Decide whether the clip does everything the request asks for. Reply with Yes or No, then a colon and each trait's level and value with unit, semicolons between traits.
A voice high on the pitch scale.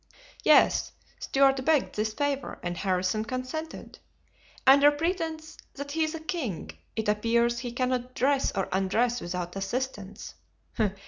Yes: very high, 255 Hz